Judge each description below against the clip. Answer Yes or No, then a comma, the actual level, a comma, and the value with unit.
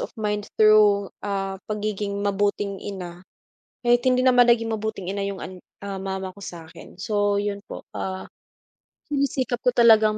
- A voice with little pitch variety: Yes, narrow, 2.3 semitones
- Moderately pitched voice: No, high, 205 Hz